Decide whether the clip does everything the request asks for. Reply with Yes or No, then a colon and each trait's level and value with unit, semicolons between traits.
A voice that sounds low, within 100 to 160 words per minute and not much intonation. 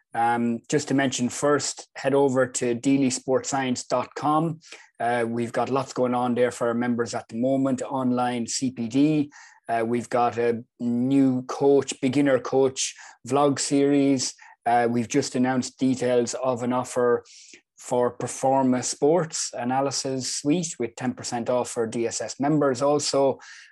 Yes: low, 125 Hz; slow, 135 wpm; narrow, 2.2 semitones